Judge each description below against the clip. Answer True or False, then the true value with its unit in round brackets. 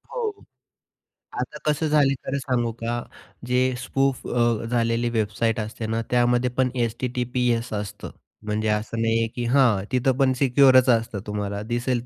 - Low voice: True (120 Hz)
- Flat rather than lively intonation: True (2.3 semitones)